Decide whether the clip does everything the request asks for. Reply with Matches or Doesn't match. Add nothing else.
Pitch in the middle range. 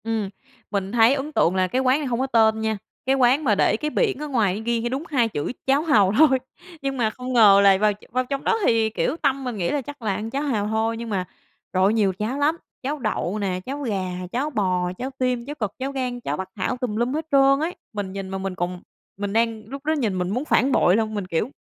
Doesn't match